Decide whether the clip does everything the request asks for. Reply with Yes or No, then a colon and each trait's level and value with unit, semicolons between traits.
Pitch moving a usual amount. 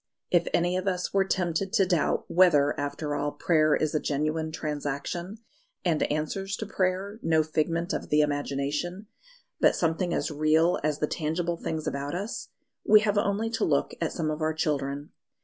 Yes: average, 3.4 semitones